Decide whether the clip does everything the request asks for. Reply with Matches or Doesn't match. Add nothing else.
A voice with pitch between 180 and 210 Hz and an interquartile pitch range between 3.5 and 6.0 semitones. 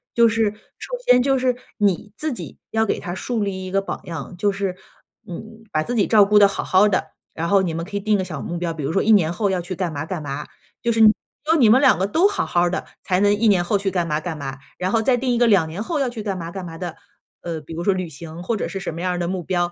Matches